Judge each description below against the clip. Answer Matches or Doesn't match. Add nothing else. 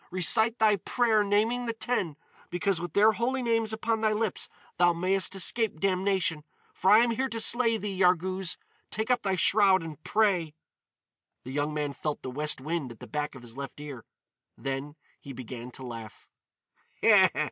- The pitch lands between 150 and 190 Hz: Matches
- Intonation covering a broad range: Matches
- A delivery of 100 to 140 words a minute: Doesn't match